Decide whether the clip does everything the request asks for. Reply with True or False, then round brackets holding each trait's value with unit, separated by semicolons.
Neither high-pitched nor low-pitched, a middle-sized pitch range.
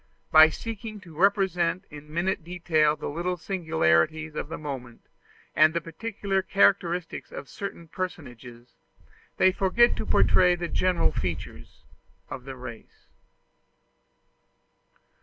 True (170 Hz; 3.9 semitones)